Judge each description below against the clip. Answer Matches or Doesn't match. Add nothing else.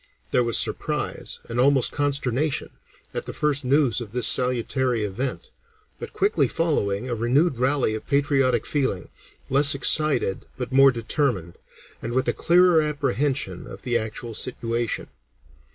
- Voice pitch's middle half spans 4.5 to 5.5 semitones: Doesn't match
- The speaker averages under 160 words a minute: Matches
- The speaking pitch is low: Matches